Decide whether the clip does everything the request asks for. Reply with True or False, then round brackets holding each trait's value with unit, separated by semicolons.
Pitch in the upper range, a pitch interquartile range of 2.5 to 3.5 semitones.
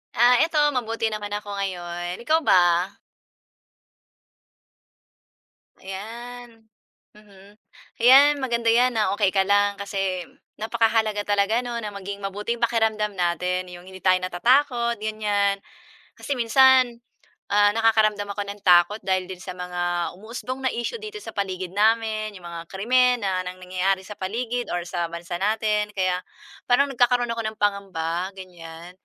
False (205 Hz; 4.0 semitones)